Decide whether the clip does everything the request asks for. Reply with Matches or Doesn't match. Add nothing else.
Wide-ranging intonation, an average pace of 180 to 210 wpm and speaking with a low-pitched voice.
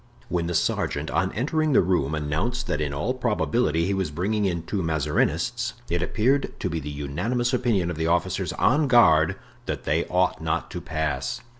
Matches